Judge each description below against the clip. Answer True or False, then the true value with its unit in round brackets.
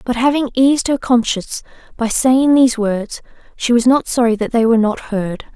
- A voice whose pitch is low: False (240 Hz)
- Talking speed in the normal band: True (195 wpm)